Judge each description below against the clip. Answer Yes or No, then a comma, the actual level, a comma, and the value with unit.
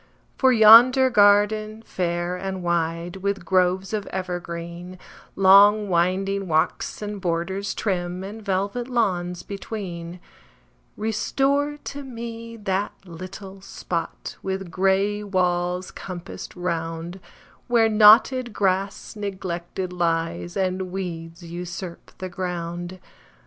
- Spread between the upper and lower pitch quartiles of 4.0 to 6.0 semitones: No, average, 2.9 semitones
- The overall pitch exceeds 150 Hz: Yes, high, 190 Hz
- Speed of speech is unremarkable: No, slow, 105 wpm